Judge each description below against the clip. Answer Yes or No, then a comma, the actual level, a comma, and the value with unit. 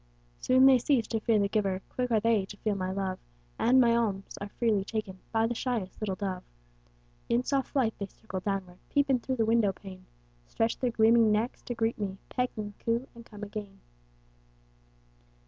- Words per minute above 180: Yes, average, 195 wpm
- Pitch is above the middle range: Yes, high, 220 Hz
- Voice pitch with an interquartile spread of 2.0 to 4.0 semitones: Yes, average, 3.1 semitones